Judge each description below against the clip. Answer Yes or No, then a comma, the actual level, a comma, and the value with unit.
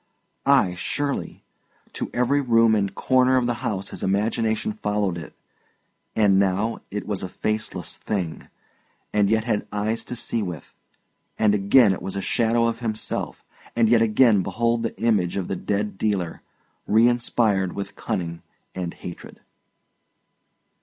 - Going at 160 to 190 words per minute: No, average, 145 wpm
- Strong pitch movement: No, average, 3.2 semitones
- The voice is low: Yes, low, 105 Hz